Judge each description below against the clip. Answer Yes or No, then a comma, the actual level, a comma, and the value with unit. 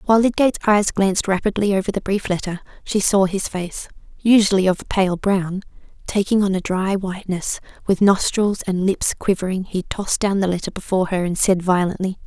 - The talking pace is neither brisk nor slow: Yes, average, 185 wpm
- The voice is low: No, high, 195 Hz